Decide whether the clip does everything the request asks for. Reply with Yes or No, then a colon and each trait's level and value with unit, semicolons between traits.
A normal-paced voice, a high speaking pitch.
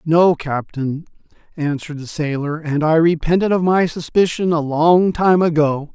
No: average, 150 wpm; medium, 160 Hz